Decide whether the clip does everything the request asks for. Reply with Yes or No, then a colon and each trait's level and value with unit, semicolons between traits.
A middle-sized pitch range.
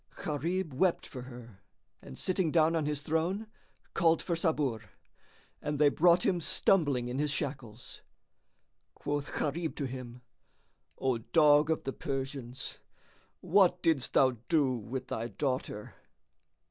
Yes: average, 4.2 semitones